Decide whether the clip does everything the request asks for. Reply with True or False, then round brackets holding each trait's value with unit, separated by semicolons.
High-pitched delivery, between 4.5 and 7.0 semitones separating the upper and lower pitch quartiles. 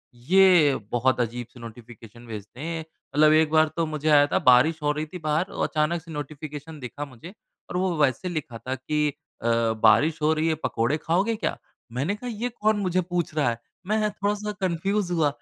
False (155 Hz; 5.4 semitones)